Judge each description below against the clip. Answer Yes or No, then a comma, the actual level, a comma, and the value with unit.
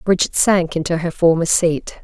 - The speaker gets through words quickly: No, average, 175 wpm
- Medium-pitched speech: Yes, medium, 170 Hz